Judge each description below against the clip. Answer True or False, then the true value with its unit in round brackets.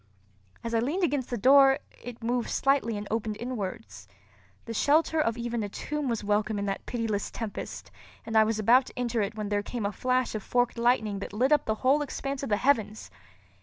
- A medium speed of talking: False (210 wpm)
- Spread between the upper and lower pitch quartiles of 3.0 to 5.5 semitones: True (3.4 semitones)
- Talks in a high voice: True (230 Hz)